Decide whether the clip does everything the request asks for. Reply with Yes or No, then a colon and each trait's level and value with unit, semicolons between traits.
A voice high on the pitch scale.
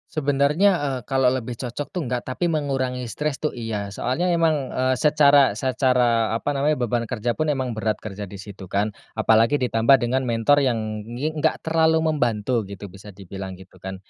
No: low, 125 Hz